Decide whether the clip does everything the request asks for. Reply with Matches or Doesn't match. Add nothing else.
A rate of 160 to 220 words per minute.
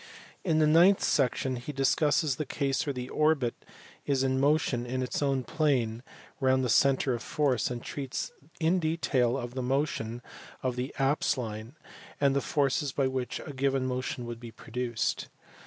Matches